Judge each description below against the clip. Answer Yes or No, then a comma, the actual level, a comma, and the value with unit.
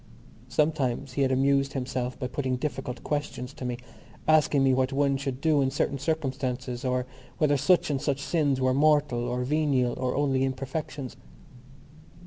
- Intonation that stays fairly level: Yes, narrow, 2.1 semitones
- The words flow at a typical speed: Yes, average, 160 wpm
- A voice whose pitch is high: No, low, 135 Hz